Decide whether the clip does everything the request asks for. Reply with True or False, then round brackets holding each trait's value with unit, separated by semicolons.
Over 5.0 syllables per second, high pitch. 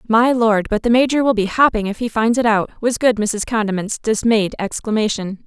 True (5.3 syllables/s; 220 Hz)